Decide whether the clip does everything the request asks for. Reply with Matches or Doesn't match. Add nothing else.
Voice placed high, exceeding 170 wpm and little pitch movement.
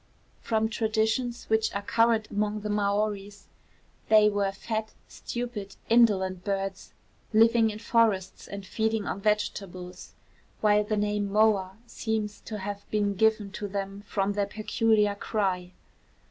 Doesn't match